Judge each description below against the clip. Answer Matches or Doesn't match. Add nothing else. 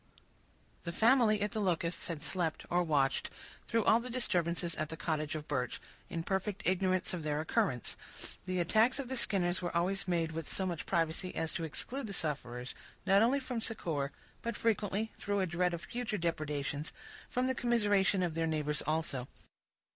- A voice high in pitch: Doesn't match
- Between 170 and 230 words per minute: Matches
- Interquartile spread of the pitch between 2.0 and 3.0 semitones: Doesn't match